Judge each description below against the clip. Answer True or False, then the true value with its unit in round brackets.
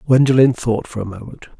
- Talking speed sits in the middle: True (190 wpm)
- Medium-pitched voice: False (120 Hz)